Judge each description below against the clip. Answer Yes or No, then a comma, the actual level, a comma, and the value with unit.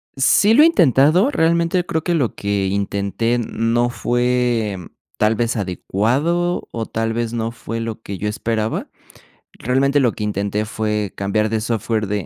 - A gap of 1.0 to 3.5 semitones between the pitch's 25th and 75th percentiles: No, average, 4.0 semitones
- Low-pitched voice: Yes, low, 115 Hz